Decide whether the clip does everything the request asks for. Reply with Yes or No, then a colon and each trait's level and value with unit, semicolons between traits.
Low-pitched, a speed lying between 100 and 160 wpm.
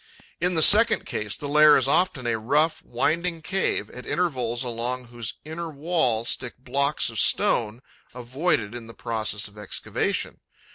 Yes: low, 125 Hz; average, 155 wpm